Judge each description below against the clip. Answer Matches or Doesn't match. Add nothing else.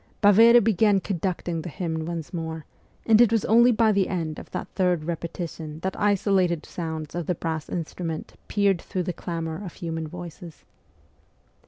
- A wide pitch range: Doesn't match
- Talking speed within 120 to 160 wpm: Doesn't match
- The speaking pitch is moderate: Matches